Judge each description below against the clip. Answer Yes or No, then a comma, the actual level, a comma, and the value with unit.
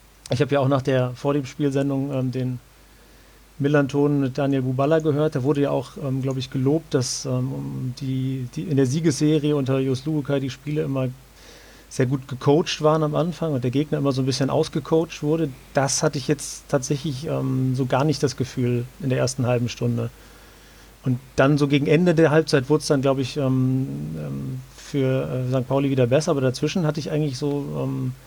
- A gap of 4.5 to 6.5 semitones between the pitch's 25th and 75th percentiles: No, narrow, 2.4 semitones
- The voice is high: No, medium, 140 Hz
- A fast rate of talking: Yes, fast, 195 wpm